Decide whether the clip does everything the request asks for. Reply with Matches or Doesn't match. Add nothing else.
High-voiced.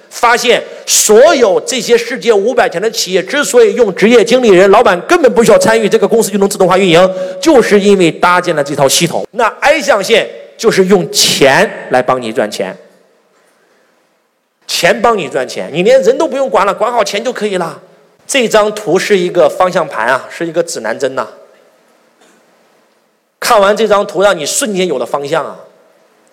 Matches